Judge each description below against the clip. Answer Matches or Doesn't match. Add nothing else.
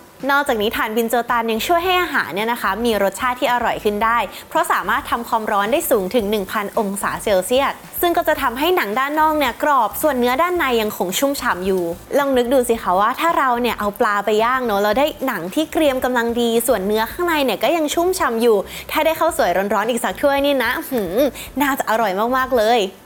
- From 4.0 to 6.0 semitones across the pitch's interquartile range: Matches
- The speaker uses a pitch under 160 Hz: Doesn't match